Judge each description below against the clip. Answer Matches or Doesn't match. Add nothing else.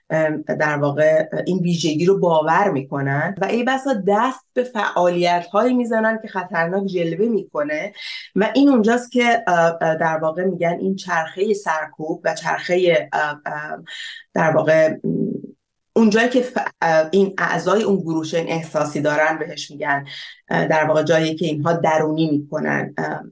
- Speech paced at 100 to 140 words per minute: Matches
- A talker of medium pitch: Matches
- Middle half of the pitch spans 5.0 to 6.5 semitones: Doesn't match